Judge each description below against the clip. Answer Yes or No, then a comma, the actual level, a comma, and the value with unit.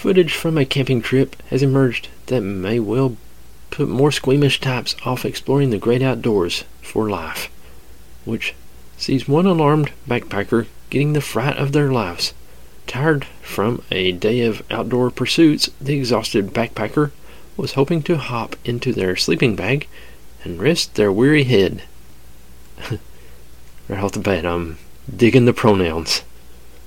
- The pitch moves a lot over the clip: Yes, wide, 8.4 semitones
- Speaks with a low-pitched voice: Yes, low, 115 Hz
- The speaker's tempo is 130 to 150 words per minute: Yes, average, 140 wpm